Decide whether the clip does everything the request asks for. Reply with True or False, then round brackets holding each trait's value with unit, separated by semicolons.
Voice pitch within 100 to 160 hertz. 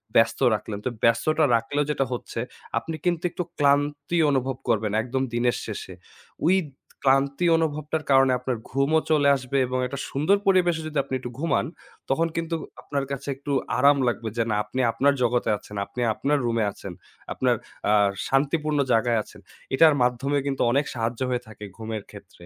True (135 Hz)